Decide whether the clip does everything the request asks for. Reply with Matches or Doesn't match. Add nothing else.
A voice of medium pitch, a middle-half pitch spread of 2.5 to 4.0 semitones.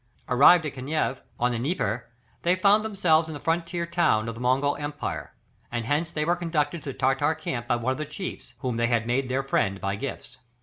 Doesn't match